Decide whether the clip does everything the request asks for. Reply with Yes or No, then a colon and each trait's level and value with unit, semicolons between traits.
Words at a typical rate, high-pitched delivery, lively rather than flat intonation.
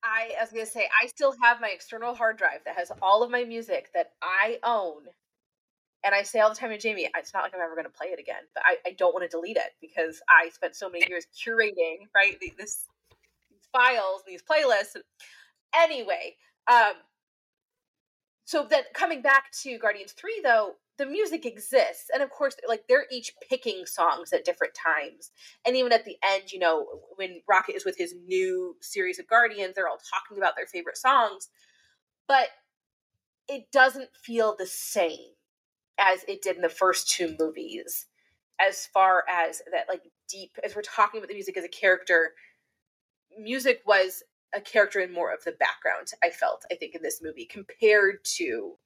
Yes: average, 190 wpm; high, 230 Hz; wide, 8.0 semitones